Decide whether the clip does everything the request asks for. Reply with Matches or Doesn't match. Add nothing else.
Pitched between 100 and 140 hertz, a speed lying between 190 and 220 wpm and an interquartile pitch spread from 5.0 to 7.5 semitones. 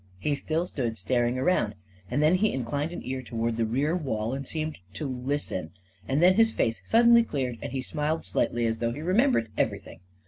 Matches